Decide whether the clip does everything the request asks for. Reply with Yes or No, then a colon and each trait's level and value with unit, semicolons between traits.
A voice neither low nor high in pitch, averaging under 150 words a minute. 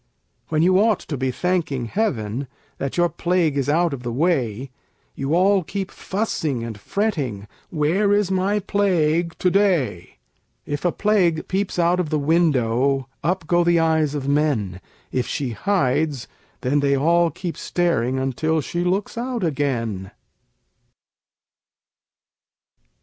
Yes: medium, 160 Hz; average, 140 wpm